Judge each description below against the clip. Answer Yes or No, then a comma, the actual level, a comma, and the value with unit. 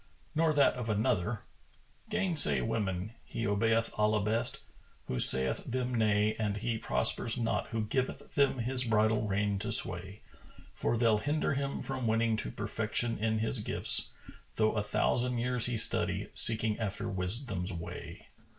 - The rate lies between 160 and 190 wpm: No, average, 150 wpm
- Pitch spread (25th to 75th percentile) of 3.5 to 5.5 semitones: No, average, 2.8 semitones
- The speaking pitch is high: No, low, 110 Hz